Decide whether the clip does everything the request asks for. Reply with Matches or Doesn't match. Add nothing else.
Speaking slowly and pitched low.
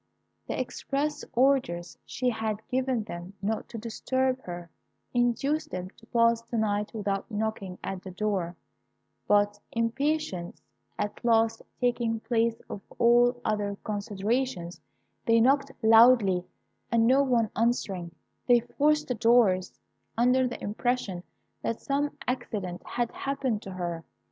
Doesn't match